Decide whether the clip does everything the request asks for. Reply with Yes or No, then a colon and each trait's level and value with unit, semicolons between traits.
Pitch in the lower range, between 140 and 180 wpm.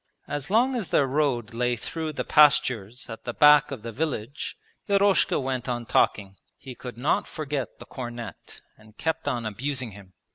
Yes: low, 130 Hz; average, 175 wpm